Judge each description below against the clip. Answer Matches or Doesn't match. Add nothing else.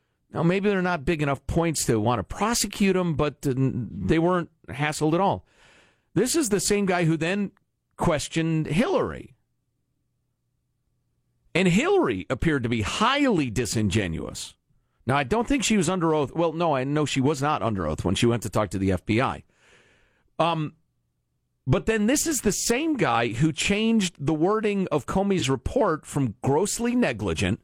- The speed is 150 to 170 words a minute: Matches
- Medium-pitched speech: Matches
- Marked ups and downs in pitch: Matches